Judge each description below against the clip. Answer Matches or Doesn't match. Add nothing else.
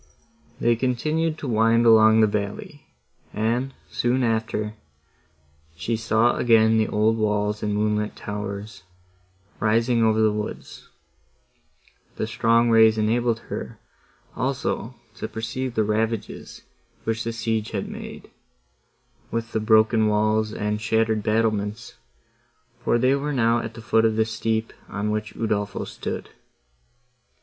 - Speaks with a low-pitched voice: Matches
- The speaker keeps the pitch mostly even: Matches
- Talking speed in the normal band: Doesn't match